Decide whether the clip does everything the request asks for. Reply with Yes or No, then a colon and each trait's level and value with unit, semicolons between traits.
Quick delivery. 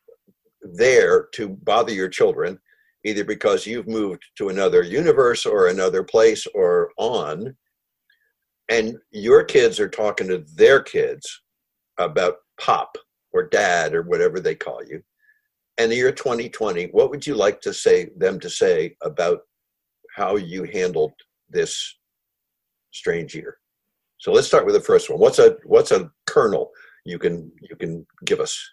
No: average, 150 wpm